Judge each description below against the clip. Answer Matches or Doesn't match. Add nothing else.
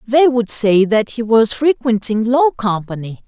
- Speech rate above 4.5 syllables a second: Doesn't match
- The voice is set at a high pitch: Matches